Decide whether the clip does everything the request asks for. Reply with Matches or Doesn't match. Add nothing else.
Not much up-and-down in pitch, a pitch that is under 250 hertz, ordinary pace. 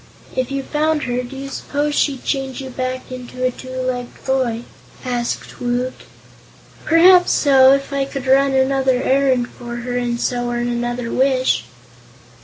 Doesn't match